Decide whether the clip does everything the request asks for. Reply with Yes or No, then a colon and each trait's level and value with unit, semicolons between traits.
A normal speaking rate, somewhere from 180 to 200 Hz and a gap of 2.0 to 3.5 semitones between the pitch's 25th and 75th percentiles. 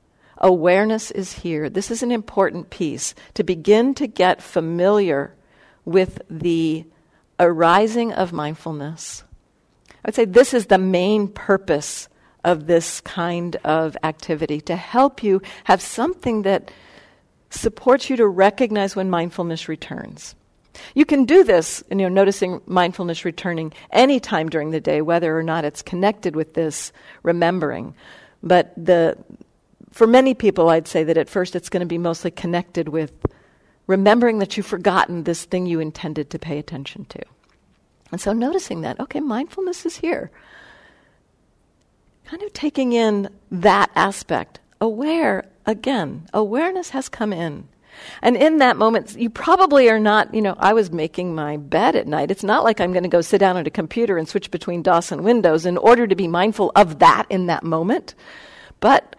No: average, 165 wpm; high, 190 Hz; average, 4.9 semitones